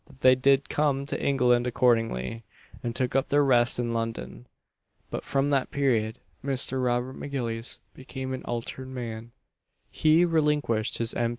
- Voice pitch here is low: Yes, low, 125 Hz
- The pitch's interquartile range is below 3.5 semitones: Yes, average, 2.8 semitones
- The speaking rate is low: No, average, 155 wpm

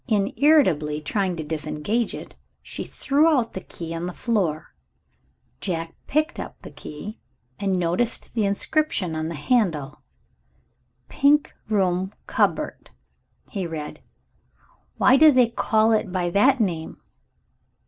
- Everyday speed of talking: No, slow, 130 wpm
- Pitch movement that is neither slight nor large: No, wide, 6.5 semitones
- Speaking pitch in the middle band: No, high, 195 Hz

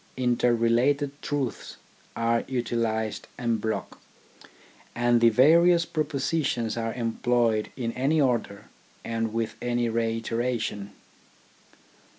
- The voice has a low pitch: Yes, low, 120 Hz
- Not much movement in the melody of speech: Yes, narrow, 2.3 semitones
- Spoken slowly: Yes, slow, 100 wpm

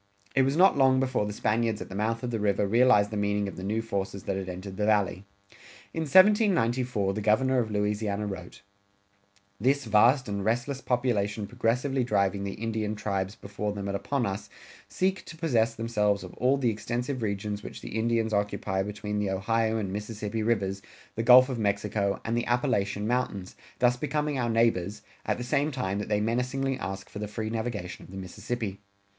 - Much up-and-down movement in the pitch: No, average, 3.4 semitones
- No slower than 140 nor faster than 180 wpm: No, average, 190 wpm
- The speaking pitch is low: Yes, low, 110 Hz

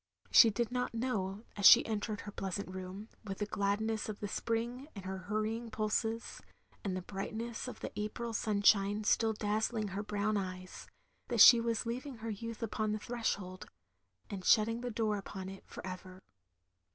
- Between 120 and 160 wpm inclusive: No, average, 190 wpm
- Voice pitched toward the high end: Yes, high, 215 Hz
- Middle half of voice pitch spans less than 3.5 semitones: Yes, narrow, 2.6 semitones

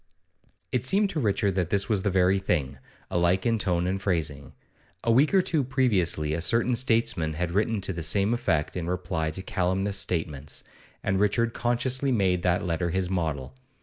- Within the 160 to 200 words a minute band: Yes, average, 180 wpm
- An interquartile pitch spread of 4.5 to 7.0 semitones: Yes, average, 4.9 semitones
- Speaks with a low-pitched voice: Yes, very low, 95 Hz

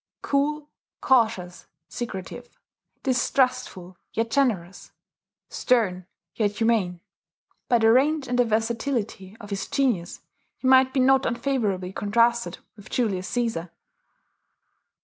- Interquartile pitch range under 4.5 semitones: No, average, 4.8 semitones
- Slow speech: Yes, slow, 110 wpm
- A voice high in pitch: Yes, high, 230 Hz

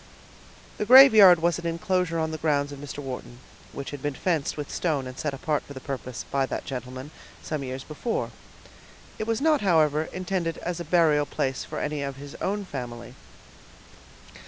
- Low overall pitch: No, medium, 150 Hz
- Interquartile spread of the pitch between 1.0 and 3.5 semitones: No, average, 4.1 semitones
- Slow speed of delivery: No, average, 180 wpm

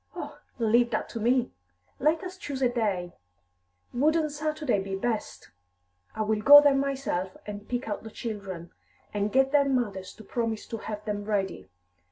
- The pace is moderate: Yes, average, 170 wpm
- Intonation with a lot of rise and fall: No, average, 4.9 semitones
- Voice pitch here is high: Yes, high, 230 Hz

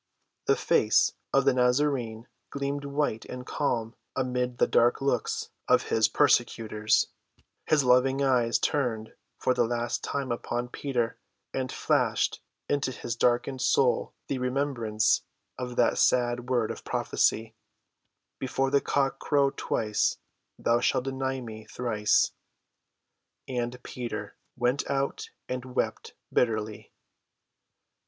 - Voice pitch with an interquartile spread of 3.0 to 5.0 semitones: No, narrow, 2.4 semitones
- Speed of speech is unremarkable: No, slow, 120 wpm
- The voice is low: Yes, low, 125 Hz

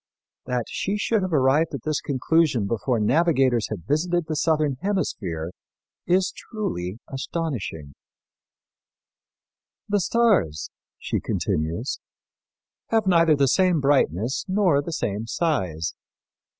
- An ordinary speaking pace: No, slow, 110 wpm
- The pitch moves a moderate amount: No, wide, 7.7 semitones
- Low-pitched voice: No, medium, 145 Hz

